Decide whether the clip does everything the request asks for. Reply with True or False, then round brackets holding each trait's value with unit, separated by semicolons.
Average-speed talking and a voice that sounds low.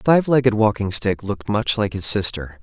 False (230 wpm; 110 Hz)